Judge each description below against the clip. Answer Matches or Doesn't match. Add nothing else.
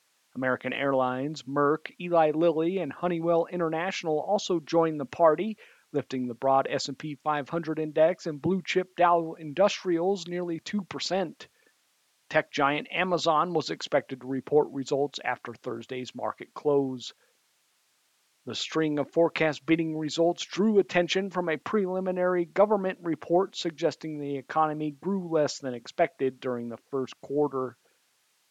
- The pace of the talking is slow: Matches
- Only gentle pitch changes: Doesn't match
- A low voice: Doesn't match